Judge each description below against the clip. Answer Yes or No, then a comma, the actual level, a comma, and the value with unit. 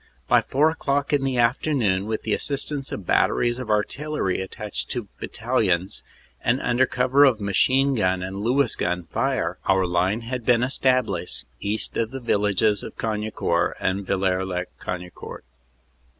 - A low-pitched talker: Yes, low, 110 Hz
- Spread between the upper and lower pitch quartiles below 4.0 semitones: No, wide, 5.4 semitones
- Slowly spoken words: No, average, 160 wpm